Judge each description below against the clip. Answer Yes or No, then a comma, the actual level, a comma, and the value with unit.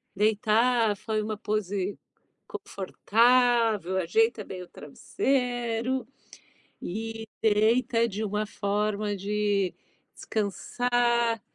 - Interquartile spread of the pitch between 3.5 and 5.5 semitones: No, narrow, 2.5 semitones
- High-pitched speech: Yes, high, 215 Hz